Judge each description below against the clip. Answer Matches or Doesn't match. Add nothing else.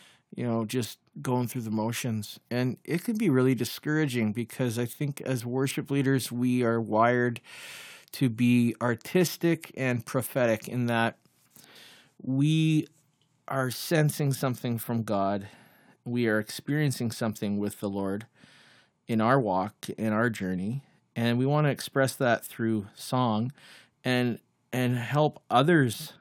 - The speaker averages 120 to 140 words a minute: Matches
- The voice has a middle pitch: Doesn't match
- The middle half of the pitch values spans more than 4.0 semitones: Doesn't match